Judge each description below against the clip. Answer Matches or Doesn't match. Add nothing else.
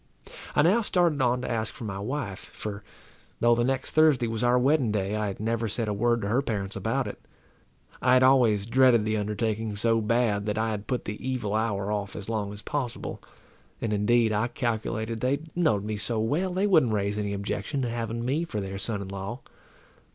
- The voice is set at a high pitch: Doesn't match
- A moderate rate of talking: Doesn't match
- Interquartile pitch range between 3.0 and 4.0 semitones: Matches